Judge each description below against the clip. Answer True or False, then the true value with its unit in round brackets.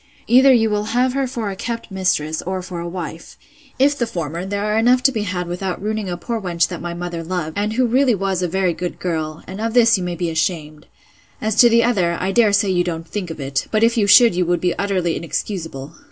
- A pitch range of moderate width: True (4.5 semitones)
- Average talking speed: False (250 wpm)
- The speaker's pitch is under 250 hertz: True (190 Hz)